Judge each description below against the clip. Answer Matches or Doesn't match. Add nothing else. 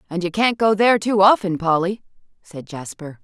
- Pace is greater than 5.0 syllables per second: Matches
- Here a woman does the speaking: Matches